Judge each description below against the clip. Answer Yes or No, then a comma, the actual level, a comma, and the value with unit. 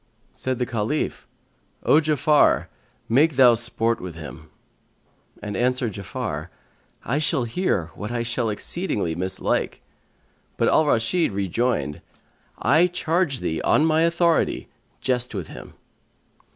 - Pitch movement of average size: No, wide, 6.7 semitones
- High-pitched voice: No, low, 125 Hz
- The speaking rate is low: Yes, slow, 125 wpm